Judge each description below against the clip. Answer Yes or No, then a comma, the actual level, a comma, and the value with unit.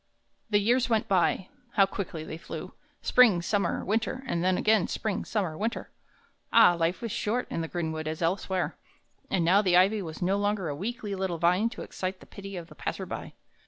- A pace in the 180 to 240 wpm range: Yes, average, 195 wpm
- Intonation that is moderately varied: Yes, average, 3.6 semitones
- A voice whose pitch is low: No, high, 190 Hz